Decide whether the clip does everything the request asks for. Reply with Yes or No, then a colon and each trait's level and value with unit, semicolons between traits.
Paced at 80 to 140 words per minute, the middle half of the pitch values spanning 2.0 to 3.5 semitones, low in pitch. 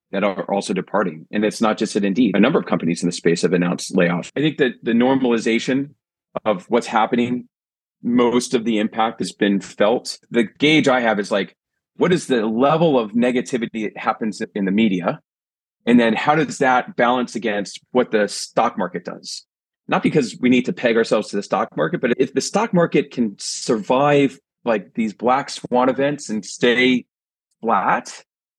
No: average, 190 wpm; average, 3.0 semitones; low, 115 Hz